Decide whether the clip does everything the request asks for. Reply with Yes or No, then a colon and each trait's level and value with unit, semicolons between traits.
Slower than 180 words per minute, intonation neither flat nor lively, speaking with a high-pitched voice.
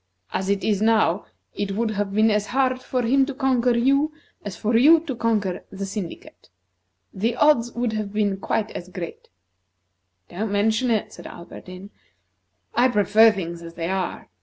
Yes: average, 170 wpm; average, 3.6 semitones; high, 215 Hz